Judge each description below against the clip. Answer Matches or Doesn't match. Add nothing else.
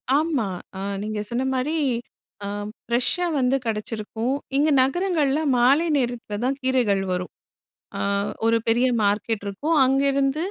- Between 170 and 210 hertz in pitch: Doesn't match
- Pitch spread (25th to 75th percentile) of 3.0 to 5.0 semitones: Matches